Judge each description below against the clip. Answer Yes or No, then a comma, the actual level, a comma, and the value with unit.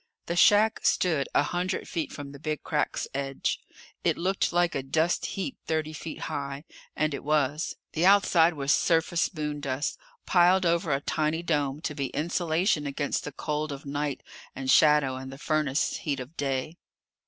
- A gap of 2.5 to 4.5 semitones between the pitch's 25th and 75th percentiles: Yes, average, 3.2 semitones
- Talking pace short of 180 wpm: Yes, average, 170 wpm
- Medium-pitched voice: Yes, medium, 150 Hz